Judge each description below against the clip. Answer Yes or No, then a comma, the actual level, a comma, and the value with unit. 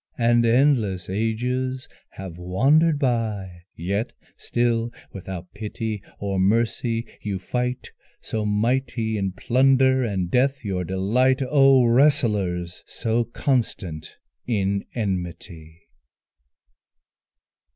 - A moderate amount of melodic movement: Yes, average, 4.8 semitones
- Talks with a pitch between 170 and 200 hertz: No, low, 110 Hz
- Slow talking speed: Yes, slow, 95 wpm